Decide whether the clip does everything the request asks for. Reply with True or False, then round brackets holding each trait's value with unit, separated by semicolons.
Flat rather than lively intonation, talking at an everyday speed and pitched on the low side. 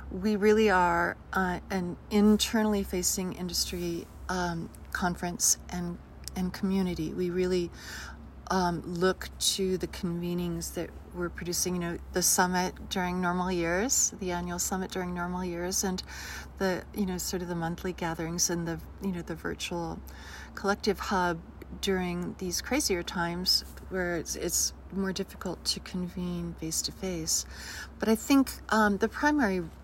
False (1.7 semitones; 145 wpm; 180 Hz)